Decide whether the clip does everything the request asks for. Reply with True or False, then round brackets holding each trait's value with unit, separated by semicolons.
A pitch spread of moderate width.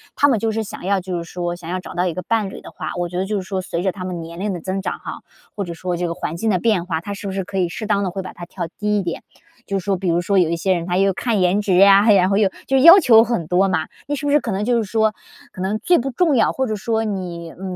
True (3.2 semitones)